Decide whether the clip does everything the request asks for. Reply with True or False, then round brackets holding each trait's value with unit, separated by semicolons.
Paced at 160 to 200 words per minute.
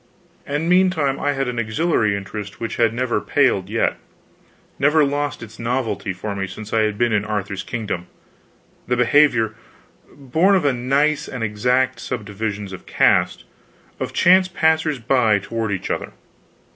False (150 wpm)